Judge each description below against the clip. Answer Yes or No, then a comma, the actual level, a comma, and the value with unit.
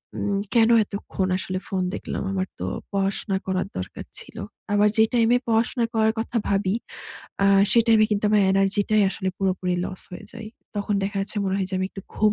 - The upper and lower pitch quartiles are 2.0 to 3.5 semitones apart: Yes, narrow, 2.4 semitones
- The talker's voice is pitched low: No, high, 200 Hz